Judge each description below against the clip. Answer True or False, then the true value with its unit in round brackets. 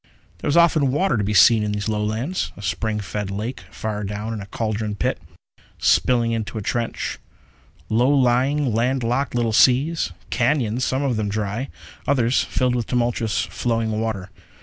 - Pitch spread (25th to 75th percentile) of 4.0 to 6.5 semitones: False (3.3 semitones)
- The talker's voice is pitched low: True (115 Hz)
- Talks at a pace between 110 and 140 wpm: False (170 wpm)